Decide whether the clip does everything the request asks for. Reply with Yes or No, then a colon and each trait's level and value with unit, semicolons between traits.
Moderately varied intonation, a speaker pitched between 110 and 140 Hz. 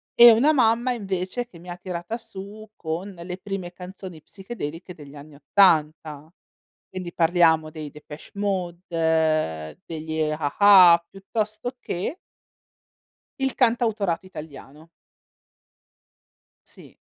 No: average, 4.3 semitones; medium, 180 Hz